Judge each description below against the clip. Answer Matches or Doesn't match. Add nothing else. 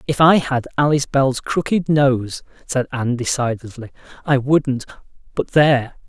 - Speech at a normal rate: Doesn't match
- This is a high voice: Doesn't match